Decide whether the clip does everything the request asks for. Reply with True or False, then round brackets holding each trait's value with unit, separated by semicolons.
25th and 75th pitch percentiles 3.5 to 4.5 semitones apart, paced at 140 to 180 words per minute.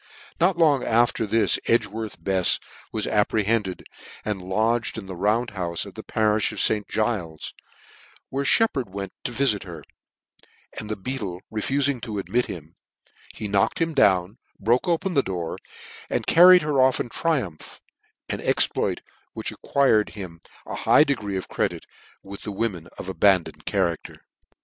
False (5.0 semitones; 160 wpm)